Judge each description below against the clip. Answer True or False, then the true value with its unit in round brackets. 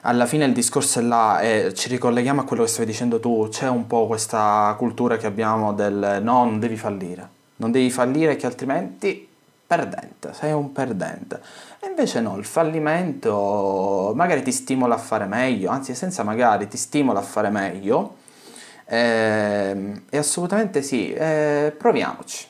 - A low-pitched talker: True (120 Hz)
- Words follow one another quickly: False (160 wpm)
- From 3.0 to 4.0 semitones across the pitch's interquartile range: False (4.7 semitones)